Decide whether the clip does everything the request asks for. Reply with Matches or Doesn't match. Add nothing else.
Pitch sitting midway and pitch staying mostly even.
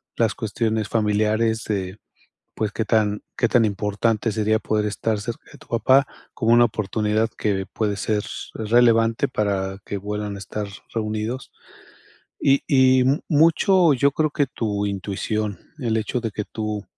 Doesn't match